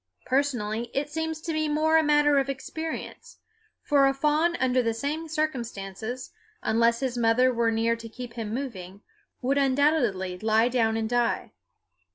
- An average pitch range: Yes, average, 4.5 semitones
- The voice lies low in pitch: No, very high, 255 Hz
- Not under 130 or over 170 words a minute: Yes, average, 160 wpm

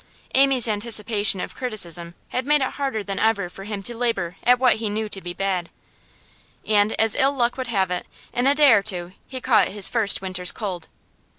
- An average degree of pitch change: Yes, average, 4.2 semitones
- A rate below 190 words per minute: No, fast, 205 wpm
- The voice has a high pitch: Yes, high, 215 Hz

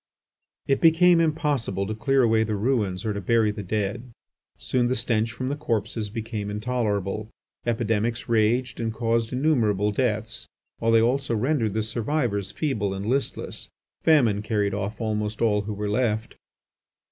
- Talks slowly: No, average, 155 wpm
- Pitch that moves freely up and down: No, average, 3.2 semitones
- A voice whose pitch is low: Yes, low, 110 Hz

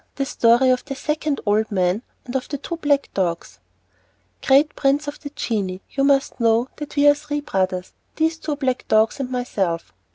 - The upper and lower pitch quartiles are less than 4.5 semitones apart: No, average, 5.0 semitones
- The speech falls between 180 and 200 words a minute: Yes, average, 190 wpm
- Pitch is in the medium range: No, very high, 265 Hz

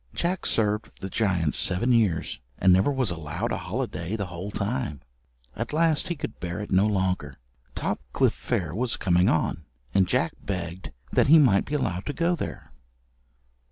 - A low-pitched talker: Yes, low, 100 Hz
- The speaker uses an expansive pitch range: Yes, wide, 5.9 semitones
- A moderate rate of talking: Yes, average, 170 wpm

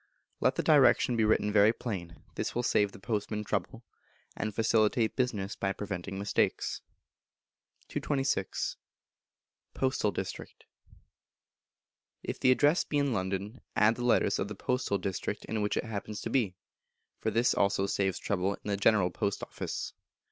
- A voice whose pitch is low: Yes, low, 105 Hz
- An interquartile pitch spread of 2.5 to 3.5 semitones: Yes, average, 3.0 semitones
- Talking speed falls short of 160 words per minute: Yes, average, 150 wpm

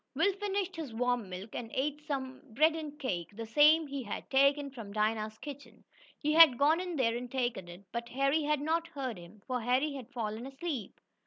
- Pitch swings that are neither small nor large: Yes, average, 4.8 semitones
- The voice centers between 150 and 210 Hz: No, very high, 265 Hz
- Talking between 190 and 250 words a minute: Yes, average, 200 wpm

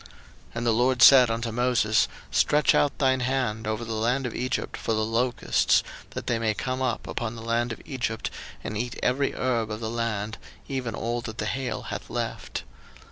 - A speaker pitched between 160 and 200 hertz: No, low, 120 Hz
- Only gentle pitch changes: Yes, narrow, 2.3 semitones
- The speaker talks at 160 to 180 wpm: No, average, 195 wpm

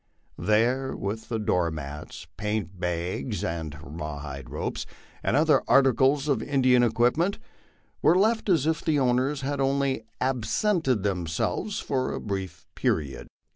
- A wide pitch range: Yes, wide, 7.7 semitones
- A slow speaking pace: Yes, slow, 130 wpm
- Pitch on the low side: Yes, low, 120 Hz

